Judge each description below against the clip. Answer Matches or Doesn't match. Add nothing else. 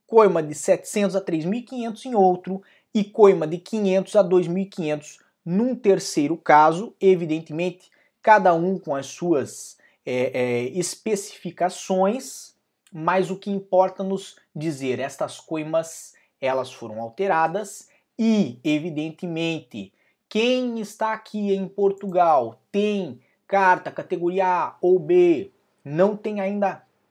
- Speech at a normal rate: Doesn't match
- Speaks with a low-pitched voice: Doesn't match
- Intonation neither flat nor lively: Matches